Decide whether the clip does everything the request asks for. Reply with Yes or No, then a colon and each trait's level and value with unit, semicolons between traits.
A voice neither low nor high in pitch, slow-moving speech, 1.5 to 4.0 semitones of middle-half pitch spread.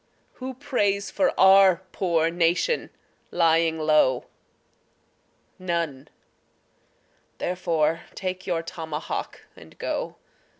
Yes: medium, 170 Hz; slow, 85 wpm; average, 2.8 semitones